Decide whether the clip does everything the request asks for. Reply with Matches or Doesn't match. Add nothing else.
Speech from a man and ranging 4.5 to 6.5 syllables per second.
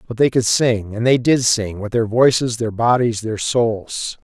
Doesn't match